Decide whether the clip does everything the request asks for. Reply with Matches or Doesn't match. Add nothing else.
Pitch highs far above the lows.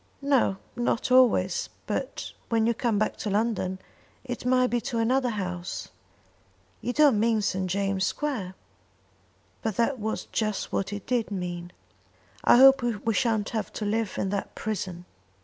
Doesn't match